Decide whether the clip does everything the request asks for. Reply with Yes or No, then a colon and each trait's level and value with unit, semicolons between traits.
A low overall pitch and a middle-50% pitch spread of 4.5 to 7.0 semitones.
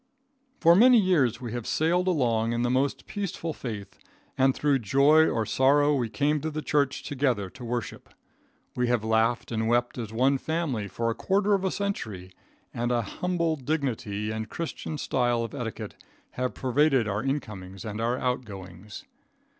Yes: low, 125 Hz; average, 5.0 semitones